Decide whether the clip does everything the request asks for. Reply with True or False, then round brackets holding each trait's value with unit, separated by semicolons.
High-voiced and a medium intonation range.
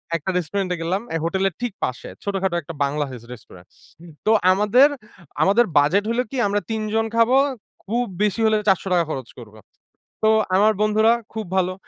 True (195 Hz; 4.5 semitones)